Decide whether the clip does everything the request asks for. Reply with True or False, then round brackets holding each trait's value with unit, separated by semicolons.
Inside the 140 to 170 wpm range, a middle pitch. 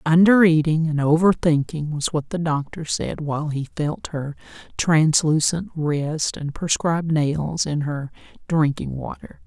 True (145 wpm; 155 Hz)